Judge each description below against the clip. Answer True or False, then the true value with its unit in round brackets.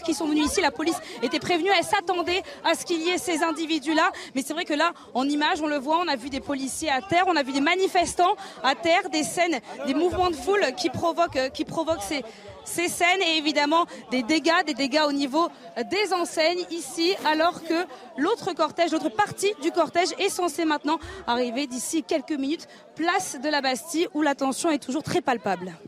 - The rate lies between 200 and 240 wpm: True (215 wpm)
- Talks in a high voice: True (325 Hz)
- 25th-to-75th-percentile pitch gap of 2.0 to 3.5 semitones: True (3.2 semitones)